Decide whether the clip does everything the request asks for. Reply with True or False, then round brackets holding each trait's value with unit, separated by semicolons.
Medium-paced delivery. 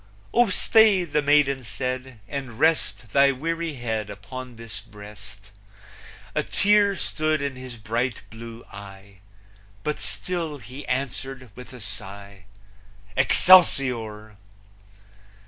False (110 wpm)